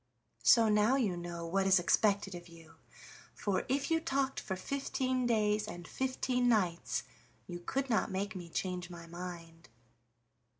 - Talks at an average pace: Yes, average, 155 wpm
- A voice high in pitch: Yes, high, 195 Hz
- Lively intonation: Yes, wide, 6.1 semitones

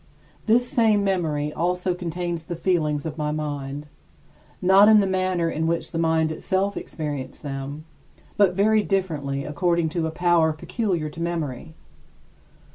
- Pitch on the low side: No, medium, 165 Hz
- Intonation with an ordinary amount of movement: Yes, average, 3.5 semitones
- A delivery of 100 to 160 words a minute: Yes, average, 145 wpm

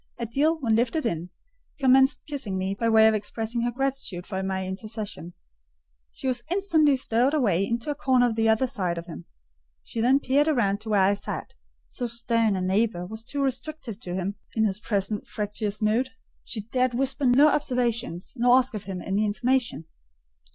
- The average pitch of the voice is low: No, high, 230 Hz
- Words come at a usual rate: Yes, average, 185 wpm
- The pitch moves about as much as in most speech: Yes, average, 4.3 semitones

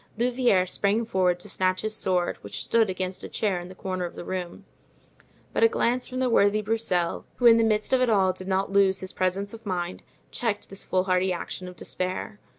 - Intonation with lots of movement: No, average, 3.3 semitones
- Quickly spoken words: Yes, fast, 215 wpm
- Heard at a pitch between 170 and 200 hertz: Yes, high, 190 Hz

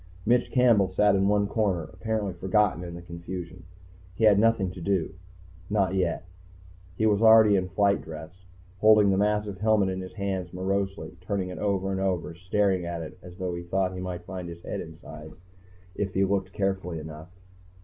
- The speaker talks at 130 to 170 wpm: No, average, 185 wpm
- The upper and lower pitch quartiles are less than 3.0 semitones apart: Yes, narrow, 2.4 semitones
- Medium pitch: No, very low, 95 Hz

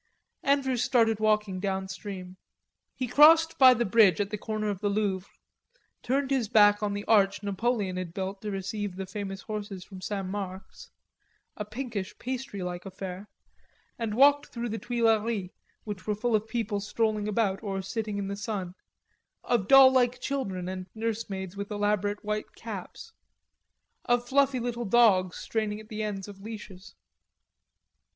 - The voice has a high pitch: Yes, high, 210 Hz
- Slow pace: No, average, 155 wpm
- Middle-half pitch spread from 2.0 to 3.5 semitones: Yes, average, 3.2 semitones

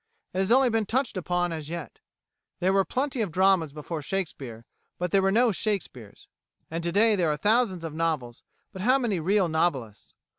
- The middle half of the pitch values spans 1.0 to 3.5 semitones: No, average, 4.8 semitones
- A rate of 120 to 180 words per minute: No, average, 190 wpm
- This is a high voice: No, medium, 180 Hz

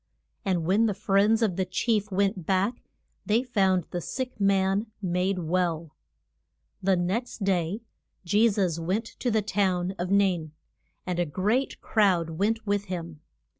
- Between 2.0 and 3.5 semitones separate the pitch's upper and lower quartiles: Yes, average, 2.9 semitones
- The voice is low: No, high, 195 Hz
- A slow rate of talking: No, average, 150 wpm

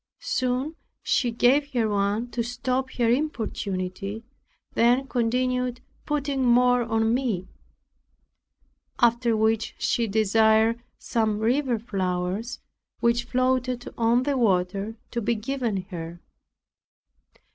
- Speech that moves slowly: Yes, slow, 105 wpm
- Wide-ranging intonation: No, narrow, 2.6 semitones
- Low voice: No, high, 235 Hz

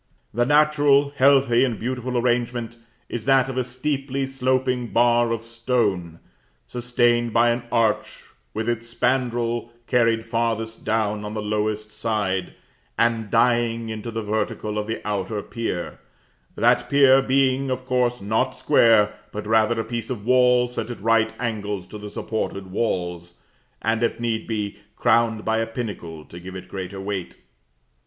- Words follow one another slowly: No, average, 155 wpm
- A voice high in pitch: No, low, 115 Hz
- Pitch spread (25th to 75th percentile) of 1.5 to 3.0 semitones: Yes, narrow, 2.6 semitones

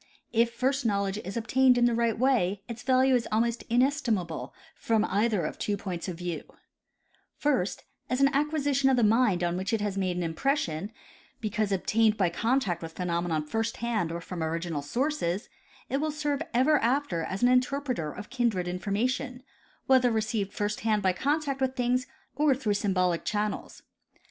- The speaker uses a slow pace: No, average, 175 wpm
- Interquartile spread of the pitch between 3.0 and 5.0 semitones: No, wide, 5.5 semitones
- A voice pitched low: No, high, 225 Hz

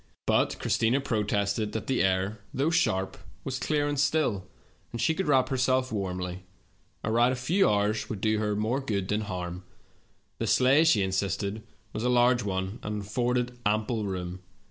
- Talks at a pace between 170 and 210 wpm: Yes, average, 175 wpm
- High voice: No, low, 110 Hz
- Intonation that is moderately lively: Yes, average, 4.3 semitones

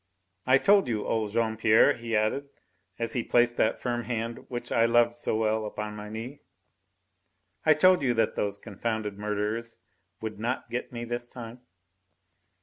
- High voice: No, low, 115 Hz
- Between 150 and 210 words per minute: Yes, average, 165 wpm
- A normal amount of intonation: No, narrow, 1.8 semitones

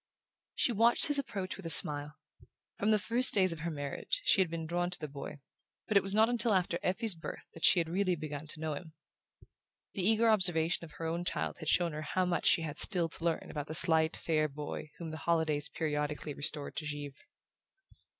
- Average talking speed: No, fast, 220 wpm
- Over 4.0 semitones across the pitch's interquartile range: No, average, 3.6 semitones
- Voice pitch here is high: No, medium, 165 Hz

